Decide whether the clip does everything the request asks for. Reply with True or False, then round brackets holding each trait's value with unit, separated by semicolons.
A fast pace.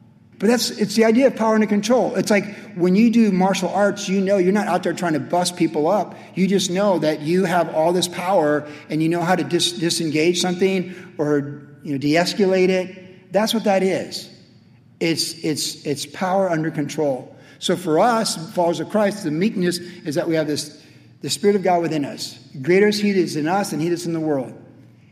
True (215 wpm)